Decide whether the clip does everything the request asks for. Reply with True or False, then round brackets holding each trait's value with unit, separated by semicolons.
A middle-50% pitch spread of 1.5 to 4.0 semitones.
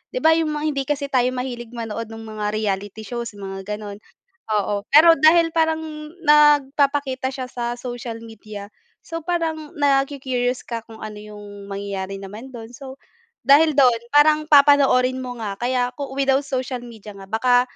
False (4.7 semitones)